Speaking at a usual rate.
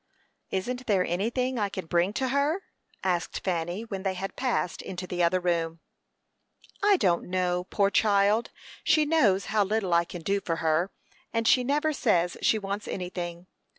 Yes: average, 170 wpm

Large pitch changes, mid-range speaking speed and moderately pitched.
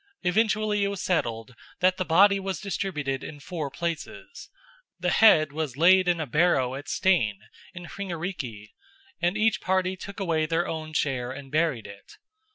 No: average, 4.8 semitones; average, 165 wpm; medium, 170 Hz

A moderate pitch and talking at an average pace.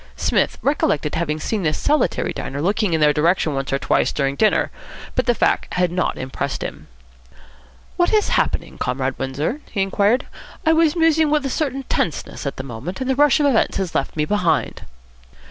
Yes: medium, 180 Hz; average, 190 wpm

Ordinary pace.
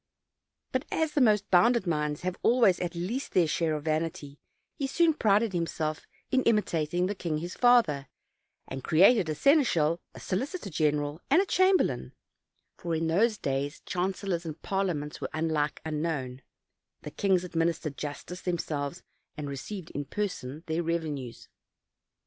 Yes: average, 150 wpm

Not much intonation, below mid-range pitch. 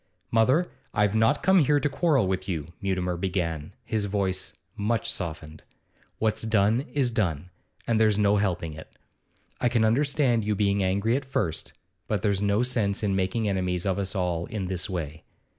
No: average, 3.5 semitones; low, 100 Hz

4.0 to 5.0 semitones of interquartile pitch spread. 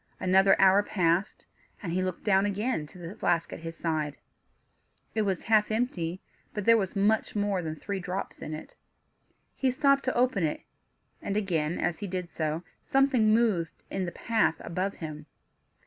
Yes: average, 4.3 semitones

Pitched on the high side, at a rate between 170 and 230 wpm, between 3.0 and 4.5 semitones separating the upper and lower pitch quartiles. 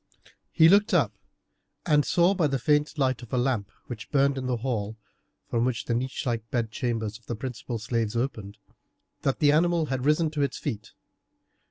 No: low, 130 Hz; average, 190 wpm; average, 4.2 semitones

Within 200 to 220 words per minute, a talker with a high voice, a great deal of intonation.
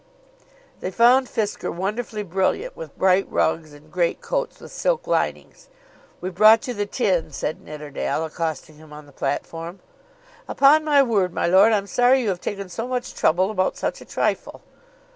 No: average, 165 wpm; high, 195 Hz; wide, 6.6 semitones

